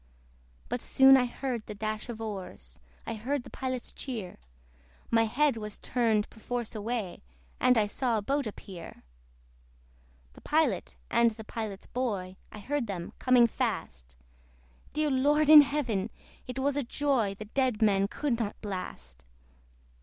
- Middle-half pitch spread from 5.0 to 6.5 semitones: No, average, 4.0 semitones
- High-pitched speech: Yes, high, 230 Hz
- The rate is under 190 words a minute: Yes, average, 150 wpm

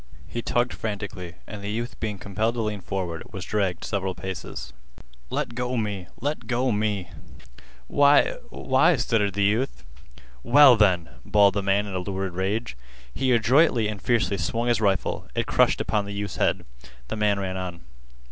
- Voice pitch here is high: No, low, 105 Hz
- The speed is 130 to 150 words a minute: No, average, 165 wpm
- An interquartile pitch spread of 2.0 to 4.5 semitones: Yes, average, 3.3 semitones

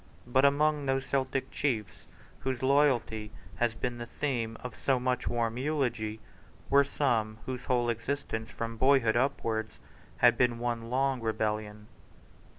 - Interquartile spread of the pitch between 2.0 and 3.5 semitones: Yes, average, 2.9 semitones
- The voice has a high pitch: No, low, 120 Hz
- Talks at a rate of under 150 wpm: Yes, average, 140 wpm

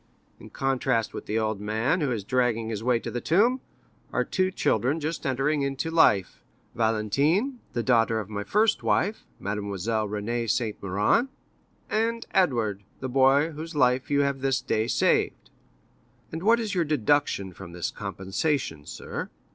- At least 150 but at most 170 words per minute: Yes, average, 155 wpm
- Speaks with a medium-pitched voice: No, low, 125 Hz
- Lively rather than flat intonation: Yes, wide, 6.4 semitones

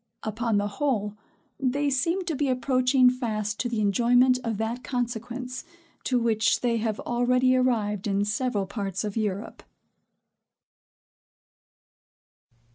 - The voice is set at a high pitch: Yes, high, 240 Hz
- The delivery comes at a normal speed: No, slow, 120 wpm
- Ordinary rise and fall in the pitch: Yes, average, 3.2 semitones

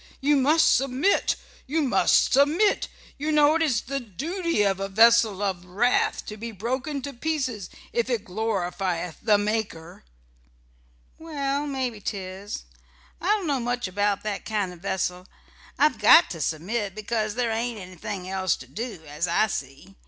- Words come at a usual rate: Yes, average, 160 wpm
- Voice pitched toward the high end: Yes, high, 220 Hz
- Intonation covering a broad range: Yes, wide, 6.1 semitones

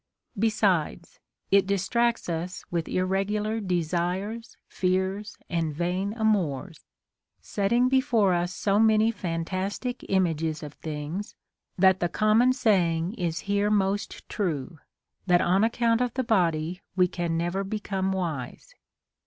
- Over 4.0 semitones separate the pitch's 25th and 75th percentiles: No, average, 3.7 semitones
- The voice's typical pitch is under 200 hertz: Yes, high, 190 Hz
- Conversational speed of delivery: No, slow, 125 wpm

